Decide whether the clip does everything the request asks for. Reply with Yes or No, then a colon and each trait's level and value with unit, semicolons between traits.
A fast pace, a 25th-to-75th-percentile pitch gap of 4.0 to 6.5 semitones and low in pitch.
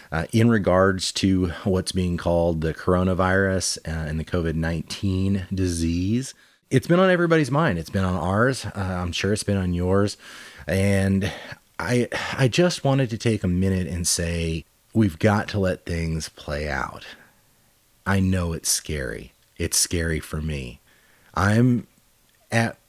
No: average, 155 wpm; average, 4.4 semitones; very low, 95 Hz